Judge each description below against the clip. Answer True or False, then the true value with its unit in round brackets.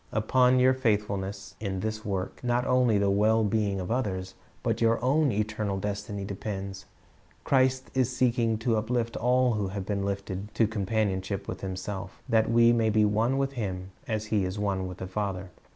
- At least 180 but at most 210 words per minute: True (185 wpm)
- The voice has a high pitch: False (105 Hz)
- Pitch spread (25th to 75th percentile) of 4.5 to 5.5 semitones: False (3.1 semitones)